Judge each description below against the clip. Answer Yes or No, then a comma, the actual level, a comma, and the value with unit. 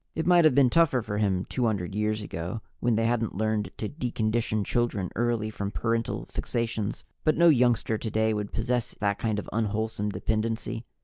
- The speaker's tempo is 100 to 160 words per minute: No, average, 175 wpm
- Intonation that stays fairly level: Yes, narrow, 2.2 semitones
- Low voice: Yes, low, 110 Hz